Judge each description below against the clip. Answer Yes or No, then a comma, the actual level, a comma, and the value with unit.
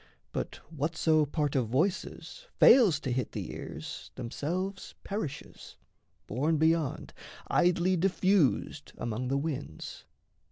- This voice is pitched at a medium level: Yes, medium, 155 Hz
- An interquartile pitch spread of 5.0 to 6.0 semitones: Yes, average, 5.3 semitones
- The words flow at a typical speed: No, slow, 110 wpm